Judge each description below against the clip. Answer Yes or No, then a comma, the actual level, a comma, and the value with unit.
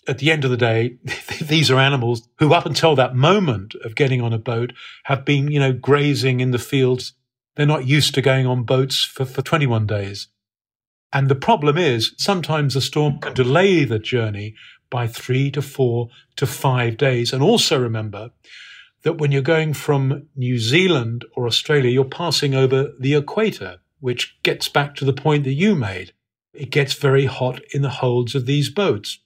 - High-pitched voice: No, low, 135 Hz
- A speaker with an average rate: Yes, average, 190 wpm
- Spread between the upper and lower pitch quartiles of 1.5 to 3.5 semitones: Yes, average, 3.1 semitones